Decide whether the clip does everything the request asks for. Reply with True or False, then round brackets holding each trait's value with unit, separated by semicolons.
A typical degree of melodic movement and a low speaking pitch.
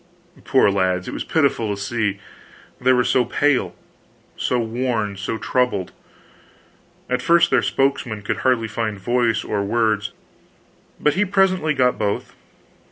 True (4.0 semitones; 115 Hz)